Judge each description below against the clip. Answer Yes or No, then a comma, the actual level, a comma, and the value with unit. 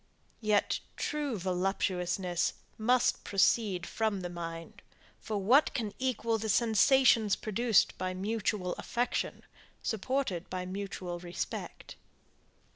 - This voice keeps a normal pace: No, slow, 105 wpm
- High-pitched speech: Yes, high, 205 Hz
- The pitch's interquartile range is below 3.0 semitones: No, average, 4.1 semitones